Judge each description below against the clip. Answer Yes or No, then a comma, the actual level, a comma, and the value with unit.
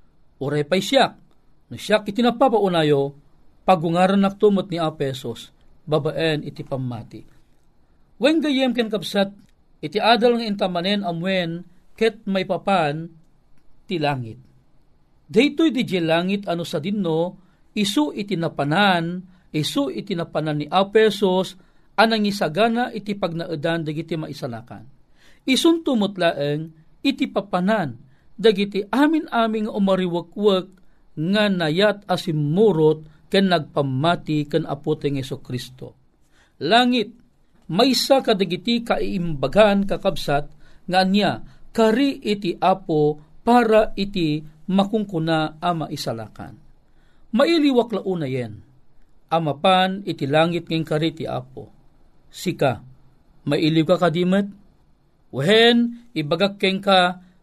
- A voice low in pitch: No, medium, 180 Hz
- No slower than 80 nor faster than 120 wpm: Yes, slow, 110 wpm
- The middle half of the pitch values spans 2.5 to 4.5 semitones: No, average, 5.1 semitones